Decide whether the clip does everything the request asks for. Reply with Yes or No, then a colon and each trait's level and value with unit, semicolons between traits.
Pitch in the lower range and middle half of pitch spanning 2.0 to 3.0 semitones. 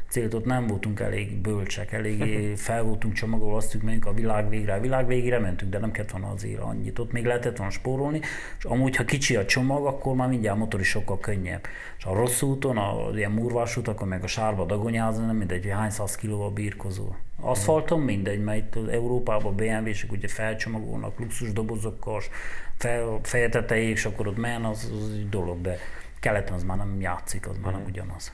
Yes: low, 110 Hz; average, 2.7 semitones